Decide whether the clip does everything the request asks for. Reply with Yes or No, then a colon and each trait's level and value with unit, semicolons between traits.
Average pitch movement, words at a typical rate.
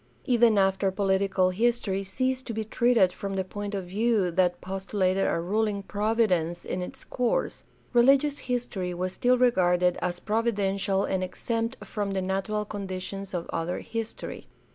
Yes: average, 3.5 semitones; average, 150 wpm